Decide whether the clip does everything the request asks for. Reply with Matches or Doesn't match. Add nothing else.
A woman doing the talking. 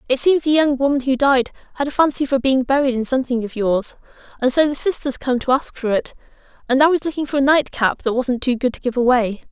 Matches